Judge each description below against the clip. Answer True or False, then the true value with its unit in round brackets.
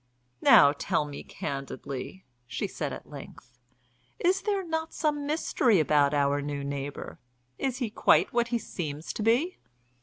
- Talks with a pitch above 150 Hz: True (185 Hz)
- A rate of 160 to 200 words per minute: False (150 wpm)